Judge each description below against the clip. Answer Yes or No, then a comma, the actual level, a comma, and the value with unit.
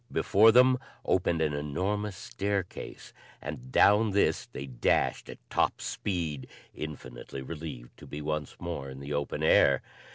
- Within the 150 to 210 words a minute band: No, average, 140 wpm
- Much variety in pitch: Yes, wide, 6.1 semitones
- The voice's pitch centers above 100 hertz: No, very low, 75 Hz